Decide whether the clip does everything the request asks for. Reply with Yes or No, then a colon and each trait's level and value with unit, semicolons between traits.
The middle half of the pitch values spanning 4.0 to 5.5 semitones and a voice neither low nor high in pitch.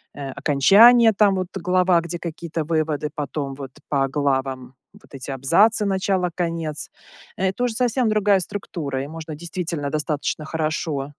Yes: average, 4.8 semitones; medium, 165 Hz